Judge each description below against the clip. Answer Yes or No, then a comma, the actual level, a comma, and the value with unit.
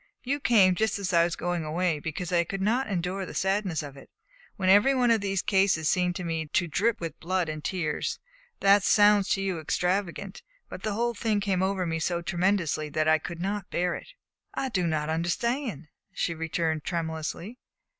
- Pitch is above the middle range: No, medium, 180 Hz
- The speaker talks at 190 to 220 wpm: Yes, average, 195 wpm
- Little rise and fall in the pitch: No, average, 3.5 semitones